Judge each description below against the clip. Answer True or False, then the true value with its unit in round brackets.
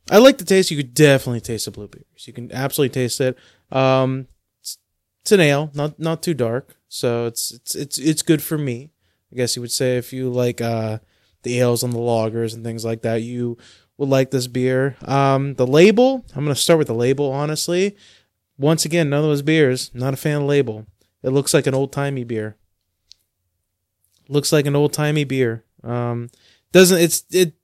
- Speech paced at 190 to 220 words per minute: True (200 wpm)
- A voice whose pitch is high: False (130 Hz)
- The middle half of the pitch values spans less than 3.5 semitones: False (4.2 semitones)